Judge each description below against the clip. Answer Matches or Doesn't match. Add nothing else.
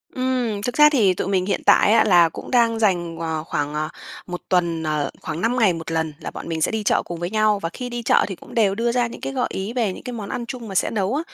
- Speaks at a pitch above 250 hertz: Doesn't match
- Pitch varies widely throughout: Matches